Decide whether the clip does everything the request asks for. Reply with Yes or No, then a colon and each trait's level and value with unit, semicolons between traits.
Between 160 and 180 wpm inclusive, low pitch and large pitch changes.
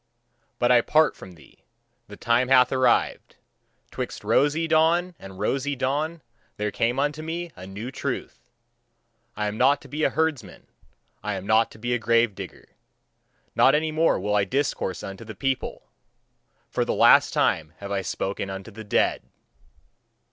Yes: average, 165 wpm; low, 120 Hz; wide, 6.2 semitones